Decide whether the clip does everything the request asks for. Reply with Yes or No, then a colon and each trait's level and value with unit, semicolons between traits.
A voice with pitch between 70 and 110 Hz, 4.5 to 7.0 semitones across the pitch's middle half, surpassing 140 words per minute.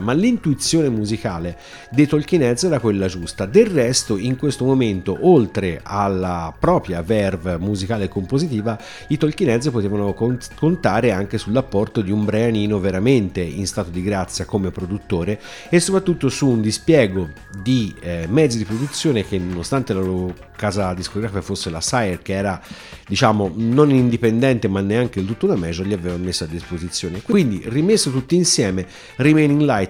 Yes: low, 105 Hz; wide, 5.6 semitones; average, 155 wpm